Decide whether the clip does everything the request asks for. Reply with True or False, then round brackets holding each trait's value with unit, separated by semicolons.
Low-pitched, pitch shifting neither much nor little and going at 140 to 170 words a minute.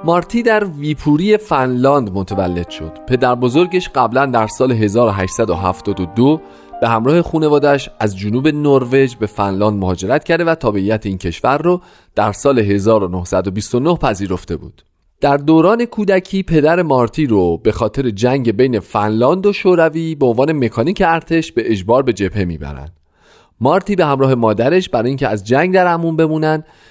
False (130 Hz; 7.4 semitones; 145 wpm)